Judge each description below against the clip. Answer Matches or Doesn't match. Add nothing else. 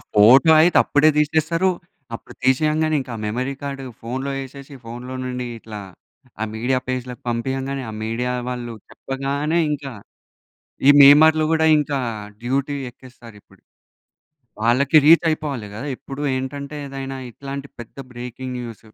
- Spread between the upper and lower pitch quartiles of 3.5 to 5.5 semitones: Doesn't match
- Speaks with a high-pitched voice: Doesn't match